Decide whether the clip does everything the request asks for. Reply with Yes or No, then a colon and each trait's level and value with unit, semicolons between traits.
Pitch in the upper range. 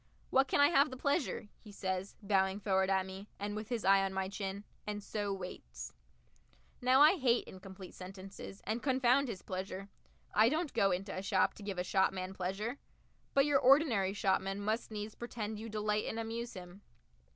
Yes: high, 205 Hz